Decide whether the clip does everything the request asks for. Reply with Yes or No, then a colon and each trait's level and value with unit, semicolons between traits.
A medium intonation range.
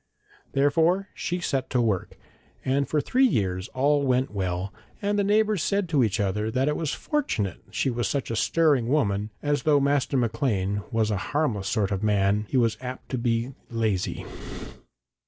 No: wide, 5.8 semitones